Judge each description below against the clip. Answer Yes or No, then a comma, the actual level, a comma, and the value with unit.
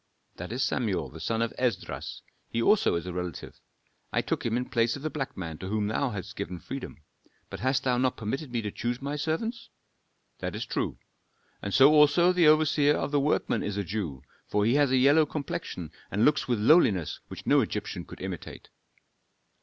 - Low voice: Yes, low, 125 Hz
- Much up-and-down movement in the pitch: Yes, wide, 6.0 semitones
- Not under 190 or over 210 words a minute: Yes, fast, 205 wpm